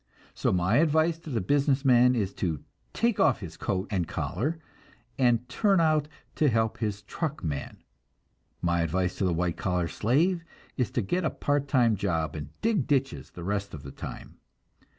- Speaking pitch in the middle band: No, low, 115 Hz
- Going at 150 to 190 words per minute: Yes, average, 180 wpm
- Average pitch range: No, wide, 8.3 semitones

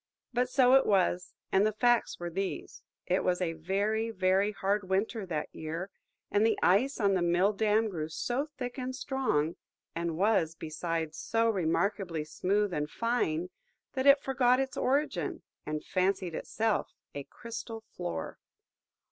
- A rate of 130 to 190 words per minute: Yes, average, 155 wpm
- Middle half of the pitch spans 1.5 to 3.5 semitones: No, average, 5.0 semitones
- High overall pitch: Yes, high, 200 Hz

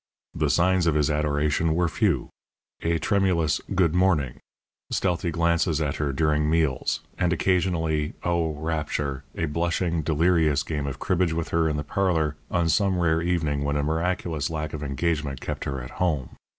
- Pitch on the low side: Yes, very low, 80 Hz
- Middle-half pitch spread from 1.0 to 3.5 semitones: Yes, narrow, 2.5 semitones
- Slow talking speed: No, average, 165 wpm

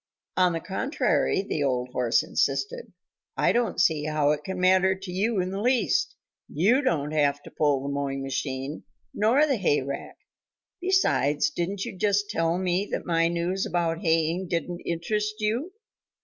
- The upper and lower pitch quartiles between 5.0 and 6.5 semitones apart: Yes, wide, 5.5 semitones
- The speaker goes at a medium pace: Yes, average, 165 wpm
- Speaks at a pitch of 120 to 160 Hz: No, medium, 175 Hz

